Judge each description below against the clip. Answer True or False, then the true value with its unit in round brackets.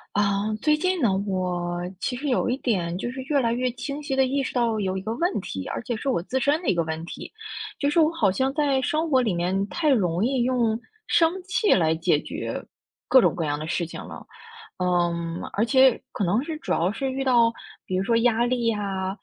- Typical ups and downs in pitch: False (6.4 semitones)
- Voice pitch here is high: True (230 Hz)